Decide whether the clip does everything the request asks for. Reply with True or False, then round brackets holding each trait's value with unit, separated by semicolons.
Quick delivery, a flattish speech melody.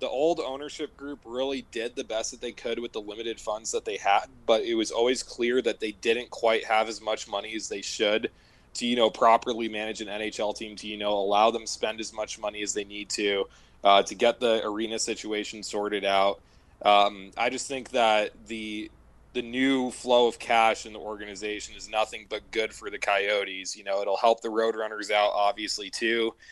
True (210 wpm; 2.3 semitones)